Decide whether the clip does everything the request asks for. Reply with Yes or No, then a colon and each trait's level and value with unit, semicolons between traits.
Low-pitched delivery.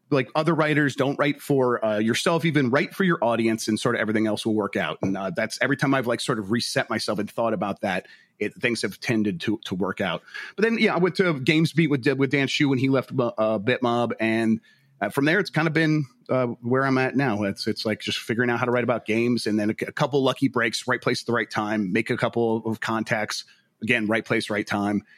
Yes: low, 120 Hz